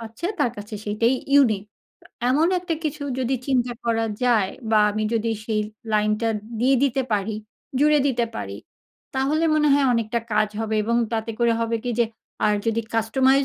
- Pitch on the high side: Yes, high, 235 Hz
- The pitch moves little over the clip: No, average, 3.6 semitones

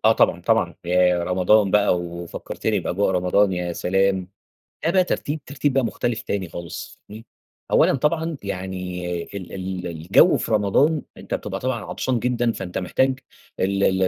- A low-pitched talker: Yes, low, 100 Hz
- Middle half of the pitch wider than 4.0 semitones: Yes, average, 5.0 semitones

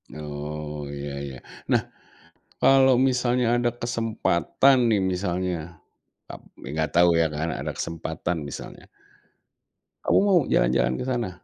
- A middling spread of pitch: No, wide, 8.2 semitones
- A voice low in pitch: Yes, very low, 90 Hz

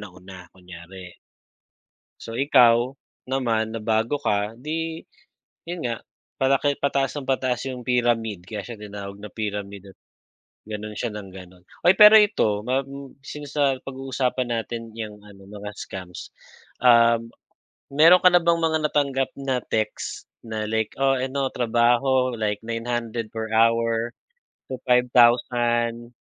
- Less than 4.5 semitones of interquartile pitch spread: Yes, average, 4.0 semitones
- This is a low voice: Yes, low, 120 Hz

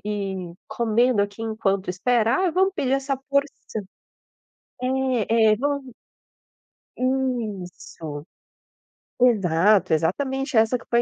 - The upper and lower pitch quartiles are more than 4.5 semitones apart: Yes, average, 4.9 semitones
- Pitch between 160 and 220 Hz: No, high, 230 Hz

